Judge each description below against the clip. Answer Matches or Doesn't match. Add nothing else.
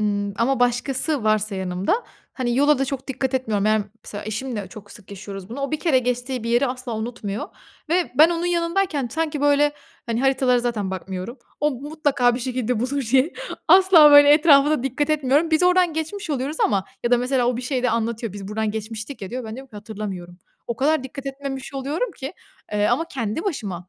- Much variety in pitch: Doesn't match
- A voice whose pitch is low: Doesn't match